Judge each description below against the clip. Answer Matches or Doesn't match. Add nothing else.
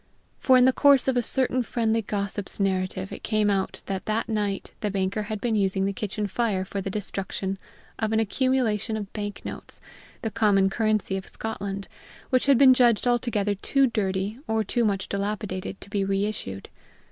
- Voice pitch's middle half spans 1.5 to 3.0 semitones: Matches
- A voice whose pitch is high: Matches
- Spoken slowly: Doesn't match